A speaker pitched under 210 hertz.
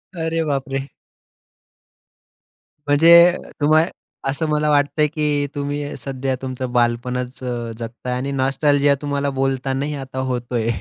Yes: low, 135 Hz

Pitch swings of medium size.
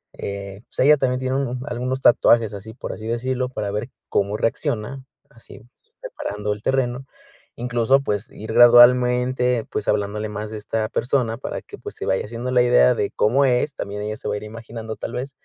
Yes: average, 3.0 semitones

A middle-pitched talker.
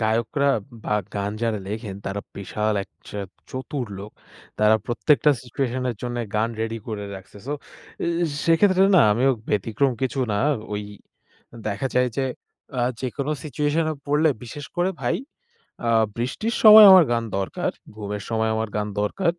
No: low, 120 Hz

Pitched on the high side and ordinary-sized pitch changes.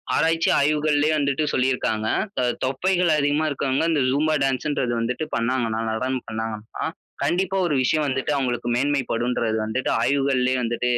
No: low, 130 Hz; average, 3.6 semitones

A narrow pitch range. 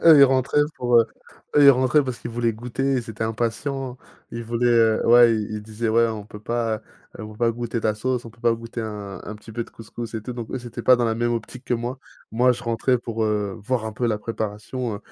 Yes: narrow, 2.0 semitones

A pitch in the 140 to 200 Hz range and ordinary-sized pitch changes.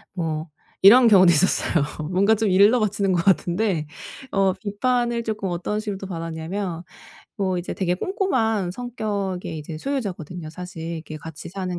Yes: high, 190 Hz; average, 3.7 semitones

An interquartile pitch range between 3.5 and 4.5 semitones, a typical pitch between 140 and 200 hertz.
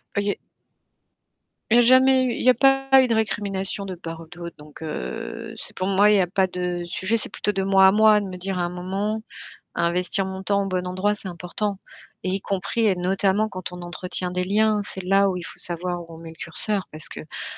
No: average, 2.7 semitones; high, 190 Hz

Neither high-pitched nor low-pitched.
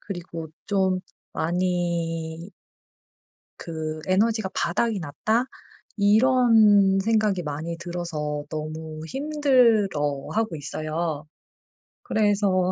Yes: medium, 180 Hz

